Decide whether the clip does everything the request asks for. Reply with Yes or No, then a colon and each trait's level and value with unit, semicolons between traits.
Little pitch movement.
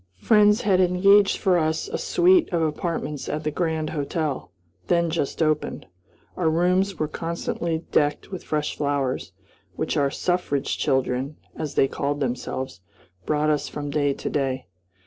No: average, 3.7 semitones